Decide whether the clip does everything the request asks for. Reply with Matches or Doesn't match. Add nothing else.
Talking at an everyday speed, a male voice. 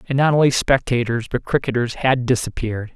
Matches